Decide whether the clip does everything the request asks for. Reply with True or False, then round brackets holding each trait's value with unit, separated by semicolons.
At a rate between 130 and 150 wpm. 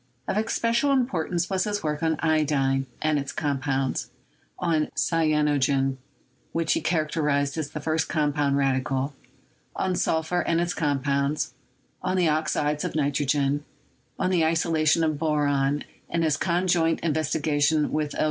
True (145 wpm)